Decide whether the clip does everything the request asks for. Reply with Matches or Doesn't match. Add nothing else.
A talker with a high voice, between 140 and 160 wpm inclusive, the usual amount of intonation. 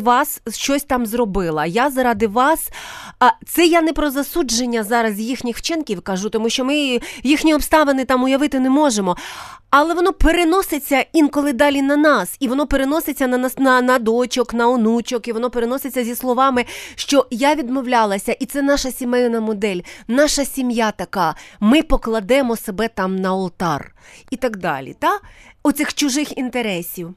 Matches